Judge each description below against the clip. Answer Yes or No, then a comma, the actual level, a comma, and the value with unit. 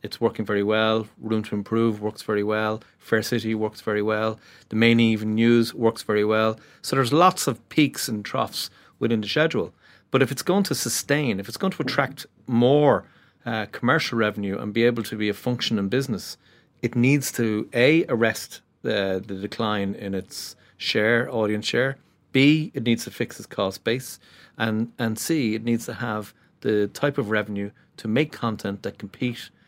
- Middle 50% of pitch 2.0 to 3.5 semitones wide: Yes, average, 3.2 semitones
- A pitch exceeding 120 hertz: No, low, 115 Hz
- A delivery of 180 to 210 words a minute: Yes, average, 190 wpm